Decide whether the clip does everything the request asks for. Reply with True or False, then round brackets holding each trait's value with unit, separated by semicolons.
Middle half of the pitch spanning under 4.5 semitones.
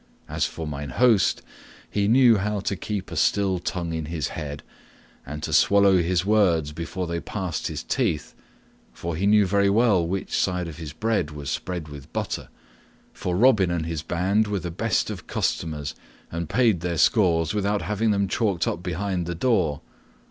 True (3.9 semitones)